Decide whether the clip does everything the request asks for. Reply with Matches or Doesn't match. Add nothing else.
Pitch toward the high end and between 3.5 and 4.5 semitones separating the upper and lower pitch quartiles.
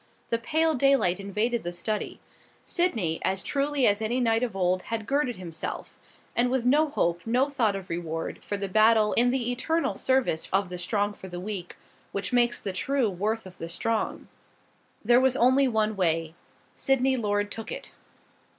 Doesn't match